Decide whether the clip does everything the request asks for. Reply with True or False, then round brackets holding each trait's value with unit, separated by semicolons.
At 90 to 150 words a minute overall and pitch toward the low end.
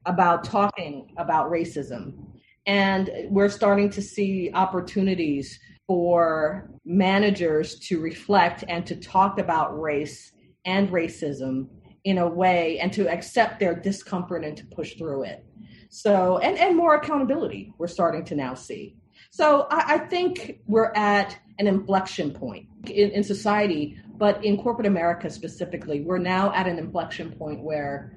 False (145 wpm; 185 Hz)